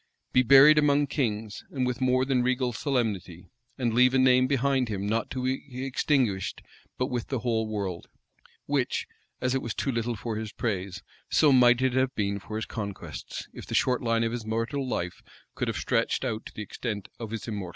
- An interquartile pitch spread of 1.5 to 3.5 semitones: Yes, average, 3.1 semitones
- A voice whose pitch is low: Yes, low, 120 Hz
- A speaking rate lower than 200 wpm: No, fast, 205 wpm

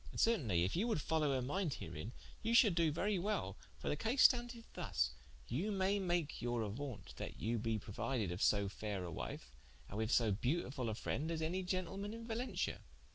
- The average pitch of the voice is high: No, medium, 150 Hz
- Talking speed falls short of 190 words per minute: No, average, 200 wpm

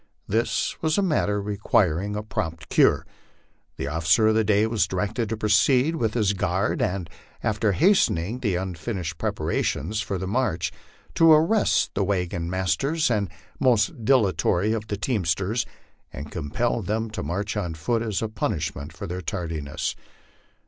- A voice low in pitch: Yes, low, 105 Hz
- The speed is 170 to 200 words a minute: No, average, 155 wpm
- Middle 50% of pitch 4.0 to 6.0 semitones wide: Yes, average, 4.4 semitones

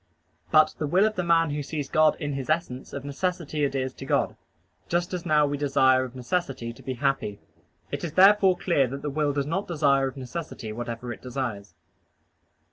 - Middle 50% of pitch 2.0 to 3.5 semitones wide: No, average, 4.1 semitones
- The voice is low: No, medium, 145 Hz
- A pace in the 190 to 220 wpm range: Yes, average, 200 wpm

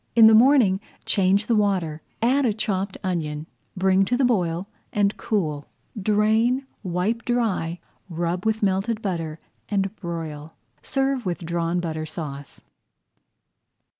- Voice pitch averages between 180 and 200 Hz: Yes, high, 190 Hz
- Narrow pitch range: No, average, 4.7 semitones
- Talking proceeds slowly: Yes, slow, 130 wpm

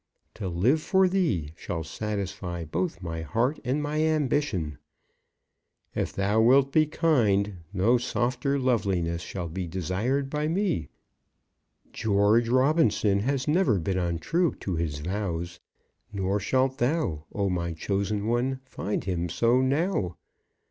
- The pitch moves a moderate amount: No, wide, 7.2 semitones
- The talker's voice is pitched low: Yes, low, 105 Hz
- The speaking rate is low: Yes, slow, 130 wpm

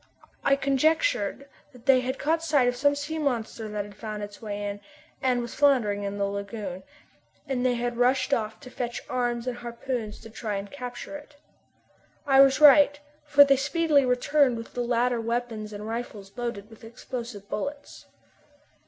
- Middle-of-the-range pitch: No, high, 245 Hz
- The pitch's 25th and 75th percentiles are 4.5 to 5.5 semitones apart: No, average, 4.1 semitones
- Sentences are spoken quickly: No, average, 180 wpm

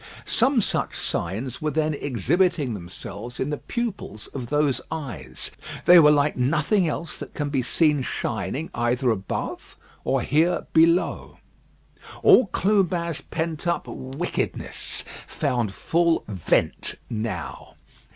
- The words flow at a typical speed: No, slow, 120 wpm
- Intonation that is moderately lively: No, wide, 5.8 semitones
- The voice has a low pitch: No, medium, 145 Hz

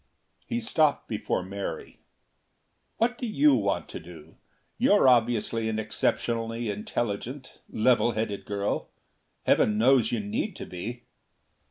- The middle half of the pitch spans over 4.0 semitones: No, average, 3.7 semitones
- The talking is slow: Yes, slow, 125 wpm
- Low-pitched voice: Yes, low, 115 Hz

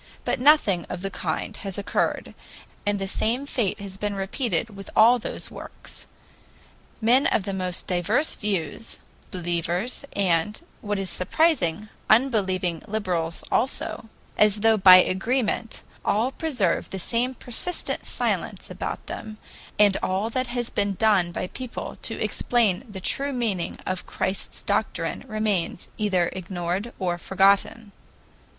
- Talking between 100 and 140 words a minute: Yes, slow, 135 wpm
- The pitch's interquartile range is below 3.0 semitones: No, average, 3.8 semitones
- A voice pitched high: Yes, high, 205 Hz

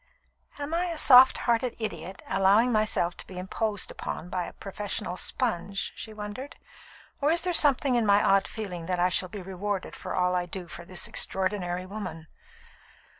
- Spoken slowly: No, average, 175 wpm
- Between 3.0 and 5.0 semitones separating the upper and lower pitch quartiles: Yes, average, 4.1 semitones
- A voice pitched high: Yes, high, 200 Hz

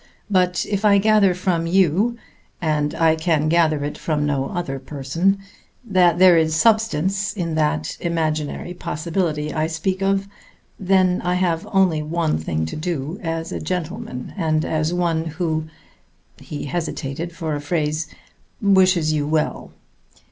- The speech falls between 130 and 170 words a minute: Yes, average, 145 wpm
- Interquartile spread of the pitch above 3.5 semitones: No, average, 3.1 semitones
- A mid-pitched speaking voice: Yes, medium, 165 Hz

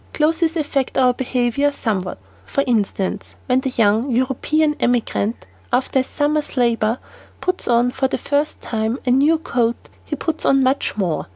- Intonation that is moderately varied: Yes, average, 3.6 semitones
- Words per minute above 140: Yes, average, 160 wpm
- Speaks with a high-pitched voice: Yes, very high, 255 Hz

